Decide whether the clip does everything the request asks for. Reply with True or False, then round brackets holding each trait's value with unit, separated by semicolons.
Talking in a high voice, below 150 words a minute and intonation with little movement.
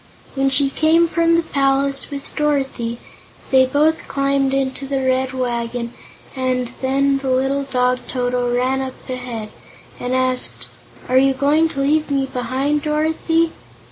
True (270 Hz; 140 wpm; 1.7 semitones)